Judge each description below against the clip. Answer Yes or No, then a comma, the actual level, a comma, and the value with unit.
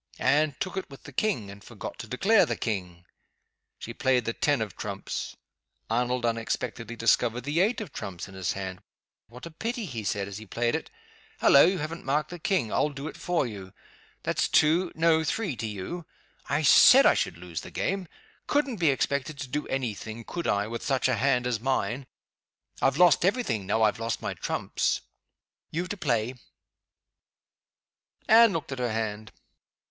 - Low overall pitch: Yes, low, 125 Hz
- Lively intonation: Yes, wide, 6.6 semitones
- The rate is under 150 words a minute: No, average, 185 wpm